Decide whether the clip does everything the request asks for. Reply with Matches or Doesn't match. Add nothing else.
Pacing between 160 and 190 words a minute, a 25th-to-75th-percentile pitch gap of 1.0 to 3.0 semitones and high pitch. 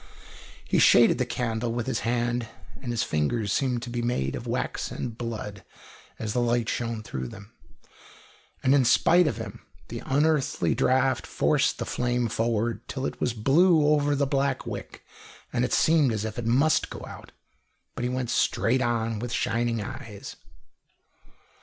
Doesn't match